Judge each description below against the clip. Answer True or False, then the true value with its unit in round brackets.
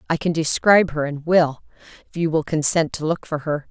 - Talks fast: True (225 wpm)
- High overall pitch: False (160 Hz)